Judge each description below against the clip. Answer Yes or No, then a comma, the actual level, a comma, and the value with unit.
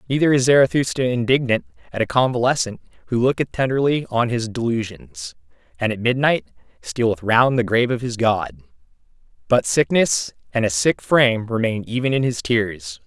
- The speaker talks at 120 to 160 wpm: Yes, average, 155 wpm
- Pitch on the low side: Yes, low, 115 Hz